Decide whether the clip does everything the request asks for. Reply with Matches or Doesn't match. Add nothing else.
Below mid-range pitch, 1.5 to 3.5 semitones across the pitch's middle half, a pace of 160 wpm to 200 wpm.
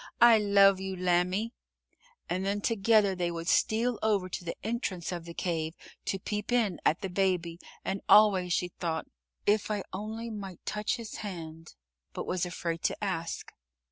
Doesn't match